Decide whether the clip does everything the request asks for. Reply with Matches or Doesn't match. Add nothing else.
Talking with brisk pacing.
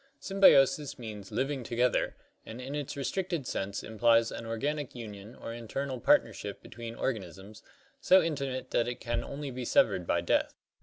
Doesn't match